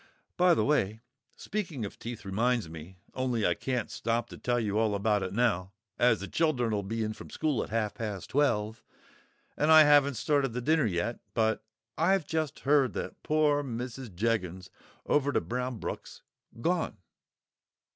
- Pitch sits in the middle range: No, low, 120 Hz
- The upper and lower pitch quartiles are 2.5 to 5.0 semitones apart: No, wide, 5.4 semitones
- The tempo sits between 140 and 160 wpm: Yes, average, 155 wpm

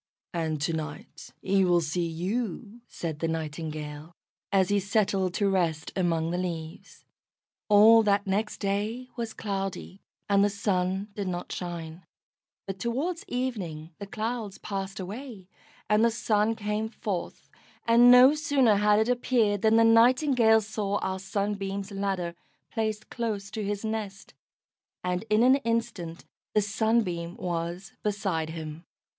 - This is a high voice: Yes, high, 200 Hz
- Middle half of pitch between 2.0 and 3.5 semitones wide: No, average, 3.9 semitones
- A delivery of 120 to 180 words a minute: Yes, average, 140 wpm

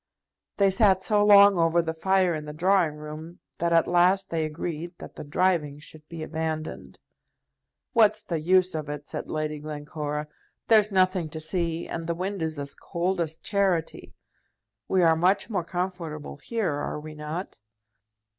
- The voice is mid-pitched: Yes, medium, 170 Hz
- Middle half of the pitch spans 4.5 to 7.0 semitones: No, average, 3.3 semitones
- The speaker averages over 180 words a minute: No, average, 165 wpm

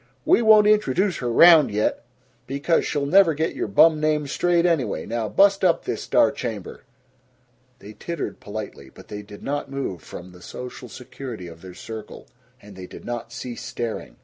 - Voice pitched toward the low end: Yes, low, 130 Hz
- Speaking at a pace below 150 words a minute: No, average, 175 wpm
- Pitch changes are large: Yes, wide, 7.5 semitones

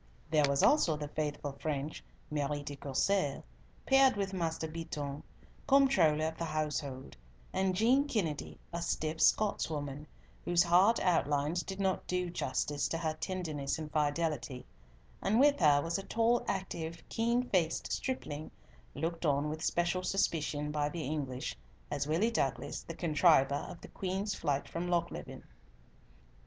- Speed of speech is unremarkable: Yes, average, 145 wpm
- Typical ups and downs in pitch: Yes, average, 4.1 semitones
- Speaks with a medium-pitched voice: Yes, medium, 160 Hz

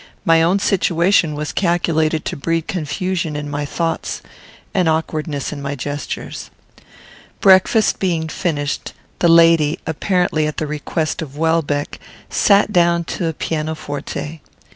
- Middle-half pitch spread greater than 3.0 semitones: No, narrow, 2.5 semitones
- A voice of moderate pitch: Yes, medium, 160 Hz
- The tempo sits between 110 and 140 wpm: Yes, slow, 135 wpm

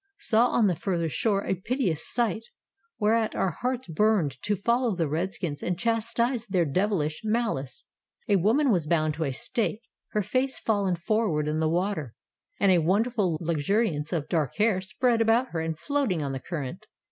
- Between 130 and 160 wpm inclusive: No, average, 175 wpm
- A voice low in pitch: No, high, 190 Hz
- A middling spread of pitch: No, wide, 6.0 semitones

